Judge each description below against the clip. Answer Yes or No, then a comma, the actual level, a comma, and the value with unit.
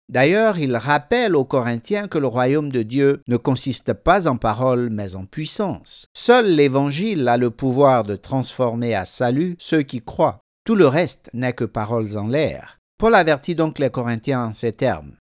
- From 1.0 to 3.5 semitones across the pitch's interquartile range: No, average, 4.0 semitones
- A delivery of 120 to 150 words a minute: No, average, 180 wpm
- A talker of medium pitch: No, low, 130 Hz